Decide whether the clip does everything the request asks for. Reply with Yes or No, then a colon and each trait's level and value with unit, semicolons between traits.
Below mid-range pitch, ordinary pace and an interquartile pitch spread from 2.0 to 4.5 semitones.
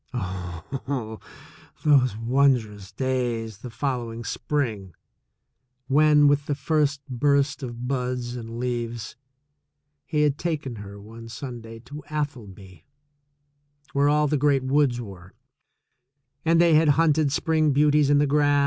No: low, 130 Hz; slow, 125 wpm; average, 4.2 semitones